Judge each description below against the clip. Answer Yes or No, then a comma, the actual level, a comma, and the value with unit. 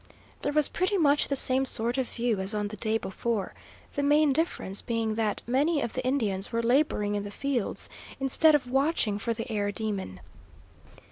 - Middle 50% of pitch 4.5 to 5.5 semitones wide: Yes, average, 5.1 semitones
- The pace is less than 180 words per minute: No, average, 190 wpm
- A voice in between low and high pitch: No, high, 235 Hz